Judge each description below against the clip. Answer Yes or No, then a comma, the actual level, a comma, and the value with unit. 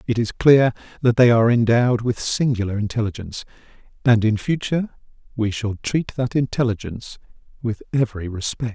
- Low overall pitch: Yes, low, 115 Hz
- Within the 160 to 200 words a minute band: No, average, 145 wpm